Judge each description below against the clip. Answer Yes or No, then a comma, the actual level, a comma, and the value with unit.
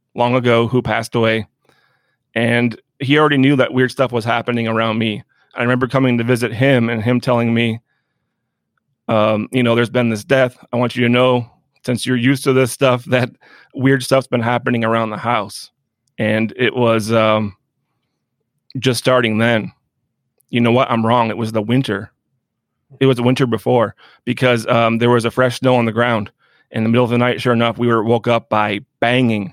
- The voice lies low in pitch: Yes, low, 120 Hz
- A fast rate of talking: No, average, 195 wpm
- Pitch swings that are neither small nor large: No, narrow, 1.9 semitones